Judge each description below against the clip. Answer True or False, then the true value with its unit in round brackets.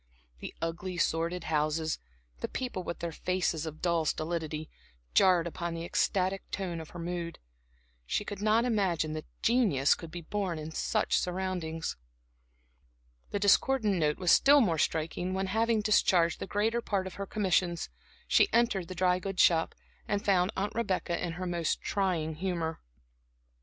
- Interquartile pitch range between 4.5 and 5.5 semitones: False (3.2 semitones)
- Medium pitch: True (180 Hz)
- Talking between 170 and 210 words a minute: False (160 wpm)